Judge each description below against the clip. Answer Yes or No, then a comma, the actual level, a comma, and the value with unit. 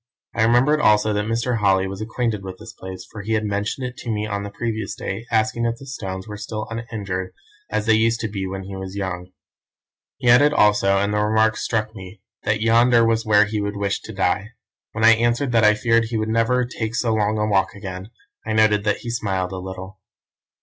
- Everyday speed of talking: No, fast, 225 wpm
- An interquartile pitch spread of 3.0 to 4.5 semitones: No, narrow, 2.4 semitones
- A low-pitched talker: Yes, low, 110 Hz